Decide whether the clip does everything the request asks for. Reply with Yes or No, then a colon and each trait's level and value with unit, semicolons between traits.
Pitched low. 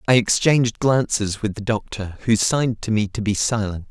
Yes: low, 110 Hz